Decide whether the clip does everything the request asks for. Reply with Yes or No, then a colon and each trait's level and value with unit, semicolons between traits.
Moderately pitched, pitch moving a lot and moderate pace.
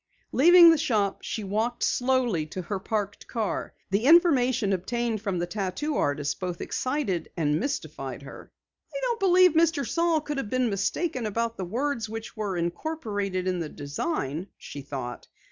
No: high, 220 Hz; wide, 7.7 semitones; average, 160 wpm